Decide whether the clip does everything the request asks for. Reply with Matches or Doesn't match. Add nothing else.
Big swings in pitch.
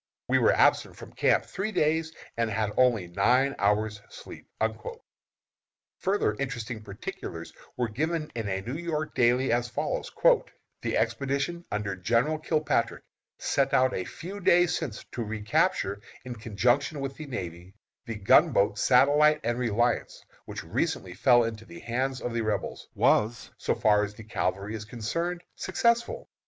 Matches